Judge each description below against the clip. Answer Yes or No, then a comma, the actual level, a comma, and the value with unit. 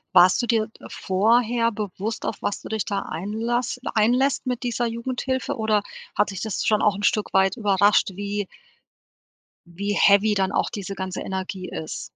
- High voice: Yes, high, 210 Hz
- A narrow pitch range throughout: No, average, 3.0 semitones